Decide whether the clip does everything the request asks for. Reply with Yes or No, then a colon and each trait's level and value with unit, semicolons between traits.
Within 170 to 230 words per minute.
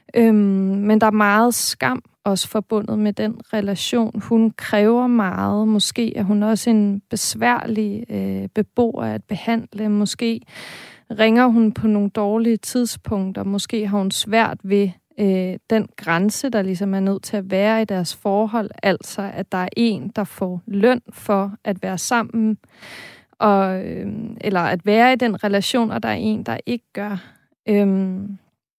No: average, 160 wpm